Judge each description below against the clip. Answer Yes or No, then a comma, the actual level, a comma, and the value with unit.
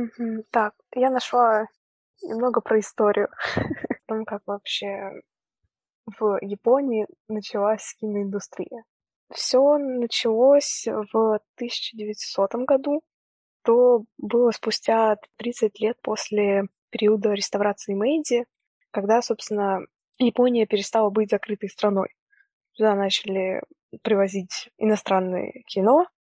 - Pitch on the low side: No, high, 220 Hz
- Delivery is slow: Yes, slow, 95 wpm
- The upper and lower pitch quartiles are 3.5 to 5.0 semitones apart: No, average, 2.8 semitones